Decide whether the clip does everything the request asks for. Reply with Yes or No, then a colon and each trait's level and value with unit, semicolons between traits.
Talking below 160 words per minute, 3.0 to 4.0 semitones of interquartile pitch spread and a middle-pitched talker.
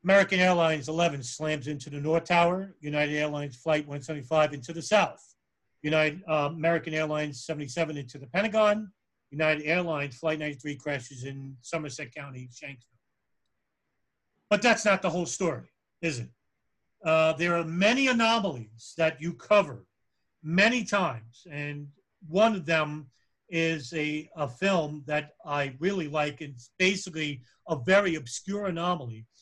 Yes: average, 140 wpm; average, 3.3 semitones; medium, 155 Hz